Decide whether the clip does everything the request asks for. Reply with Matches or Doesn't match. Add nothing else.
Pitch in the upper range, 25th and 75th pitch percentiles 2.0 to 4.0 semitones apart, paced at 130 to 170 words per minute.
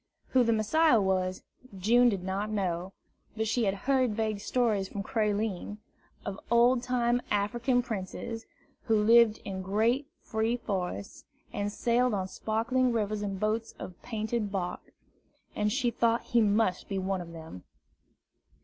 Matches